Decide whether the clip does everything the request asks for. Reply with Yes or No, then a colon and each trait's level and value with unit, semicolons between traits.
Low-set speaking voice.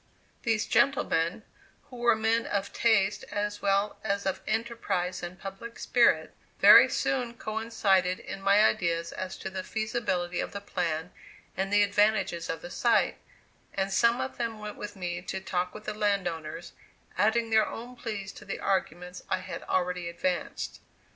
No: high, 200 Hz